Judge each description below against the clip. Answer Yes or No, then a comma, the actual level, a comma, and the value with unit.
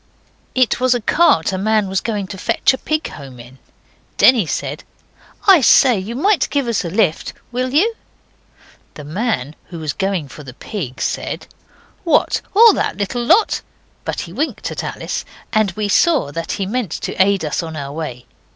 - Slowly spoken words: No, average, 185 wpm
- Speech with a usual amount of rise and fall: No, wide, 7.9 semitones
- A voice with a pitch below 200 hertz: No, high, 205 Hz